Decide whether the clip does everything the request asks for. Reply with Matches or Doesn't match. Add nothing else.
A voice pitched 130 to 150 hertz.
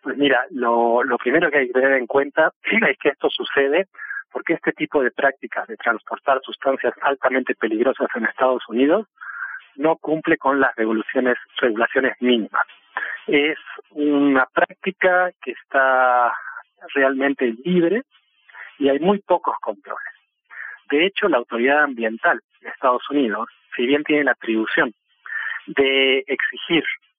Matches